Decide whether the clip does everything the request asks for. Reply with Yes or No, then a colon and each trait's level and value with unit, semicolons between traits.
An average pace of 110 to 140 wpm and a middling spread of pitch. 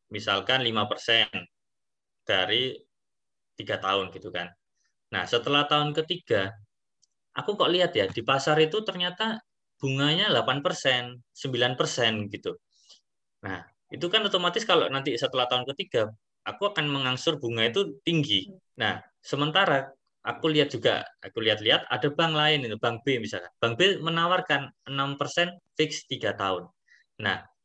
No: average, 130 wpm; wide, 5.8 semitones